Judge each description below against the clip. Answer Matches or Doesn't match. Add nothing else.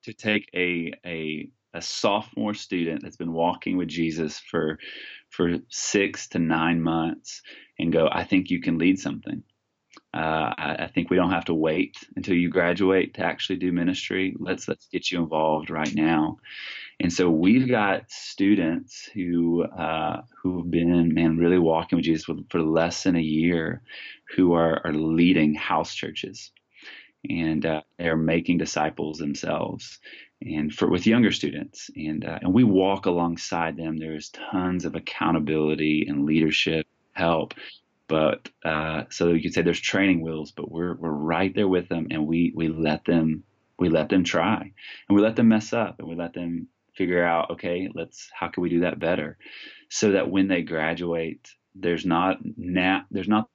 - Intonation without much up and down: Matches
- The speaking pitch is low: Matches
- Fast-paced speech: Doesn't match